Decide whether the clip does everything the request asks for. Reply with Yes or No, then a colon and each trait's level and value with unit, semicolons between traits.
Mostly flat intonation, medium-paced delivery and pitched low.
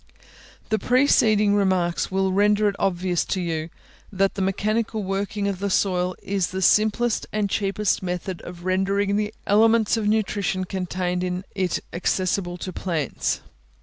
No: narrow, 2.2 semitones; average, 150 wpm; high, 195 Hz